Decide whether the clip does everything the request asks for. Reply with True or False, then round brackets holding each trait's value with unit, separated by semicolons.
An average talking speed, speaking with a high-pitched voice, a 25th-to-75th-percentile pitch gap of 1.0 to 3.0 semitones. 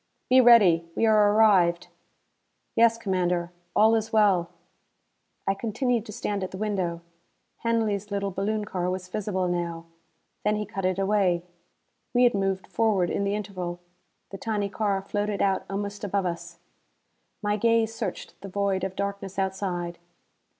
True (150 wpm; 200 Hz; 2.5 semitones)